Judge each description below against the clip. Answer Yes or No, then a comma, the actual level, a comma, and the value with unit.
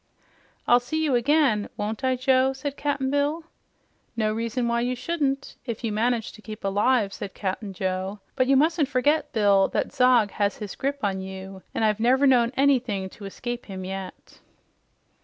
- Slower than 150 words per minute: No, average, 175 wpm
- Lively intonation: No, average, 4.7 semitones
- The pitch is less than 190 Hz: No, high, 240 Hz